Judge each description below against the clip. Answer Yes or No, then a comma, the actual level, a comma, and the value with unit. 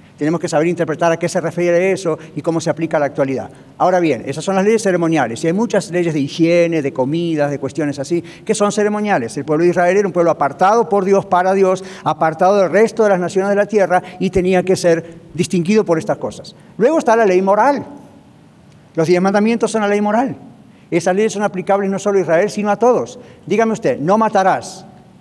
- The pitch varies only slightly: No, average, 3.7 semitones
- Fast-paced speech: Yes, fast, 220 wpm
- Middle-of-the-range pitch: Yes, medium, 180 Hz